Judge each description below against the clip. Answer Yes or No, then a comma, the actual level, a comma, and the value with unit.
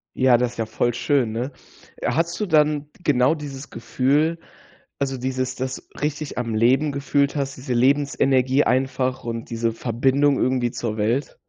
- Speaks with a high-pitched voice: No, low, 130 Hz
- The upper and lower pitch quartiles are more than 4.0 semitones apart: No, average, 2.8 semitones